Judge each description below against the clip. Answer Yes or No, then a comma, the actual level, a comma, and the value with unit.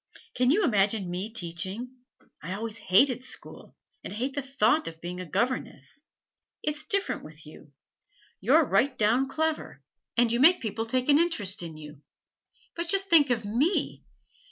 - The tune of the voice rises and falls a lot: Yes, wide, 7.0 semitones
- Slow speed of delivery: No, average, 165 wpm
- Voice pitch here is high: Yes, high, 235 Hz